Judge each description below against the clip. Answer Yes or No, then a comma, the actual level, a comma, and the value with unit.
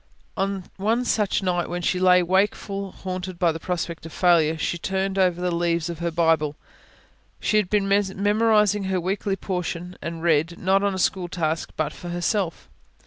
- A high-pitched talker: No, medium, 180 Hz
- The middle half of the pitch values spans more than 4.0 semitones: No, narrow, 2.5 semitones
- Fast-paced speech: No, average, 180 wpm